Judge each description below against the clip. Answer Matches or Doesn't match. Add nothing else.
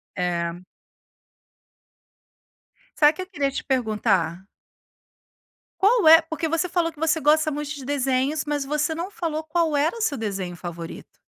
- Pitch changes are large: Matches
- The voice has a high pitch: Matches